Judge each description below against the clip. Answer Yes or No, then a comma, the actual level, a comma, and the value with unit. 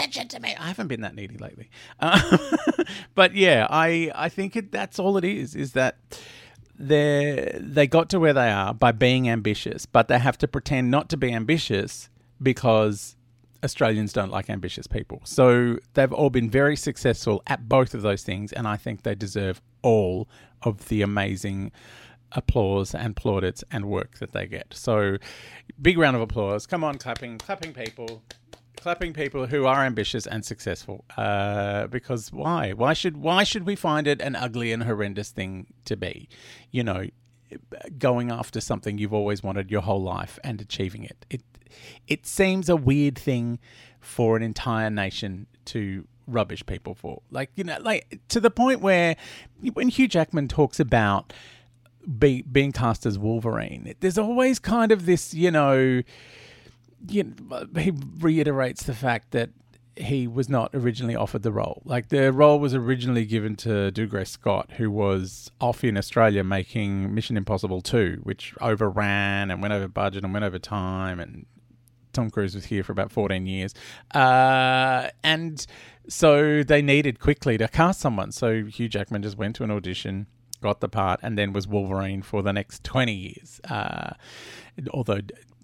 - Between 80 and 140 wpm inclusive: No, average, 170 wpm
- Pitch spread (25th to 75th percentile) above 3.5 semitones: Yes, average, 5.2 semitones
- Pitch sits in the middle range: No, low, 120 Hz